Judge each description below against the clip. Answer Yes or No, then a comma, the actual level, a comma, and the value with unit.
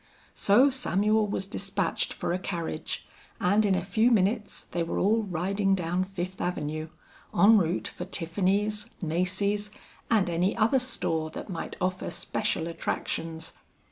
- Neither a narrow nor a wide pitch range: Yes, average, 3.3 semitones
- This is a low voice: No, high, 190 Hz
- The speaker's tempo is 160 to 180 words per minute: No, average, 140 wpm